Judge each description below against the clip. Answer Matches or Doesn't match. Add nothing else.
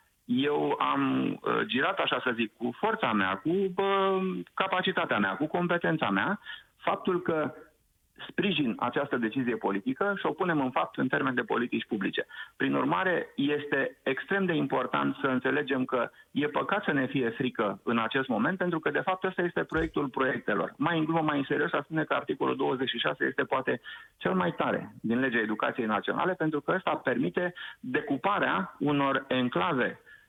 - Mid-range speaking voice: Matches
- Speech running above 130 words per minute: Matches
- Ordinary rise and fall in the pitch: Doesn't match